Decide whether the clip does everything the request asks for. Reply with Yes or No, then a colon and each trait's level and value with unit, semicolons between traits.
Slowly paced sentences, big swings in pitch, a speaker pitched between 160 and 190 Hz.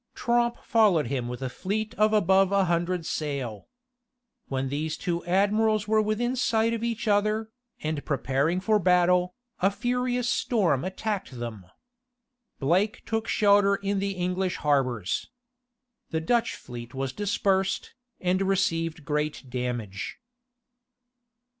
Yes: slow, 130 wpm; wide, 6.5 semitones; medium, 185 Hz